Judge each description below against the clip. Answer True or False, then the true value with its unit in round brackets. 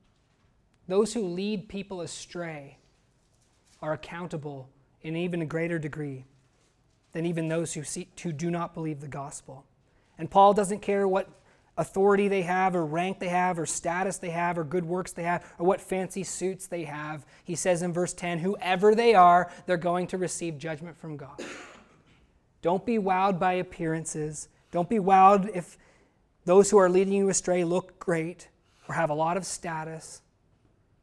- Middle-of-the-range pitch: True (170 Hz)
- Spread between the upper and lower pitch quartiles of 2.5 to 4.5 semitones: True (3.4 semitones)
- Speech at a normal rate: True (170 wpm)